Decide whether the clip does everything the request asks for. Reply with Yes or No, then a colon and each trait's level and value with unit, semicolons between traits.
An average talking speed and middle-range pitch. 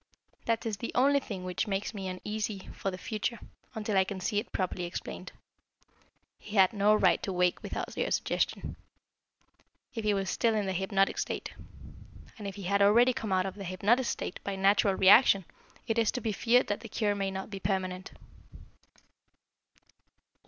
No: average, 185 wpm; high, 200 Hz